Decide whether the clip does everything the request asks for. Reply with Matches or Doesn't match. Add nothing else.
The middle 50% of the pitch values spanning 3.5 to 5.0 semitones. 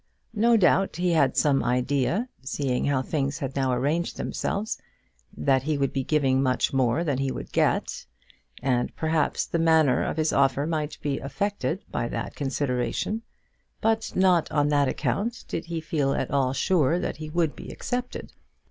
Matches